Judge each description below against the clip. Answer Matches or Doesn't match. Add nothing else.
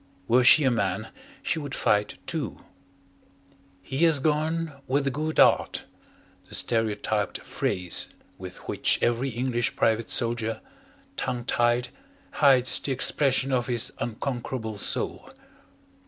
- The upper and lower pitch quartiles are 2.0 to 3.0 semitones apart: Doesn't match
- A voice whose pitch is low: Matches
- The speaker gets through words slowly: Matches